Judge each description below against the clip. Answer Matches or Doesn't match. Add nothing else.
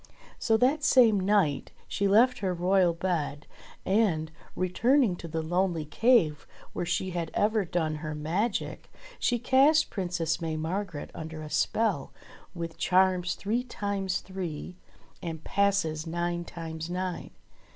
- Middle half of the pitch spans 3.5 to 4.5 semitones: Matches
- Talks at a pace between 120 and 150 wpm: Matches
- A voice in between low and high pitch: Matches